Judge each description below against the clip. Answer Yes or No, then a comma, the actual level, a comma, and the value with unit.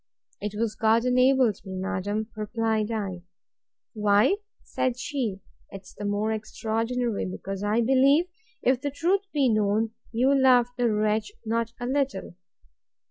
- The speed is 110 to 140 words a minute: Yes, slow, 135 wpm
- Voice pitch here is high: Yes, high, 225 Hz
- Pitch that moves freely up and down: No, average, 3.4 semitones